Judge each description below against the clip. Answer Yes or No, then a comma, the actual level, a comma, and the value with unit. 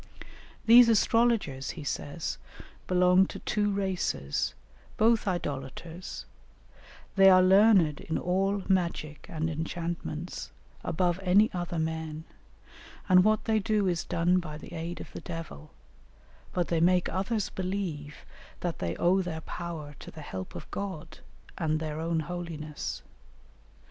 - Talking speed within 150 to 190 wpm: No, slow, 135 wpm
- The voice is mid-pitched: Yes, medium, 175 Hz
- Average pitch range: Yes, average, 3.3 semitones